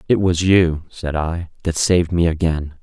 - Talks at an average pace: Yes, average, 190 wpm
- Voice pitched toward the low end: Yes, very low, 85 Hz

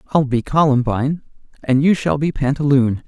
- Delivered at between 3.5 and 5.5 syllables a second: Yes, 5.1 syllables/s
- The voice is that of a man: Yes, male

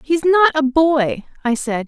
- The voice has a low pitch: No, very high, 290 Hz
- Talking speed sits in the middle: No, fast, 225 wpm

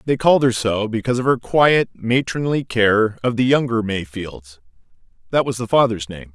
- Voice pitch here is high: No, low, 115 Hz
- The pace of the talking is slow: No, average, 170 wpm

